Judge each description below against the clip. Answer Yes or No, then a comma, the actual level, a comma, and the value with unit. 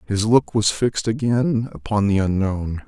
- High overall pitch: No, low, 105 Hz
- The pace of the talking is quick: No, average, 165 wpm